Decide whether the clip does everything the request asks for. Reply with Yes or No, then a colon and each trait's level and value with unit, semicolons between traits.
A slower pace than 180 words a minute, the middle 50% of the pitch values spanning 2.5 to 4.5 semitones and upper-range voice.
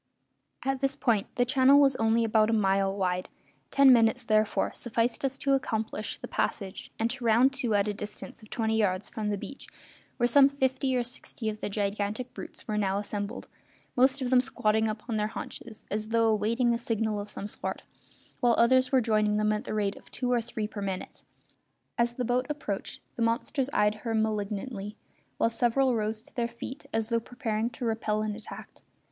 No: average, 200 wpm; average, 2.8 semitones; high, 225 Hz